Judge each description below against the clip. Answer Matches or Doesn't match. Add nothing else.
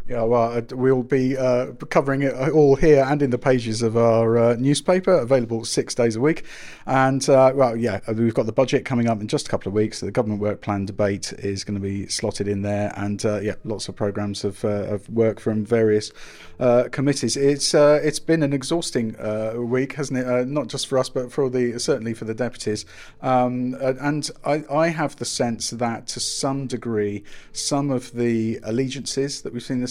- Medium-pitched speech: Doesn't match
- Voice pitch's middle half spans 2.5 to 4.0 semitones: Matches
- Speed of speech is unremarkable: Doesn't match